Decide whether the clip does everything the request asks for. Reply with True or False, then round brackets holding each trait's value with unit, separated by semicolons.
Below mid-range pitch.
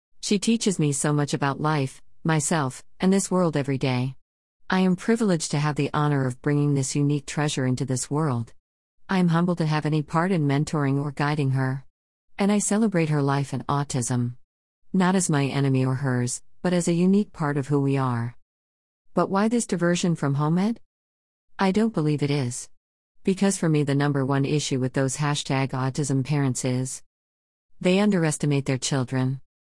False (145 Hz)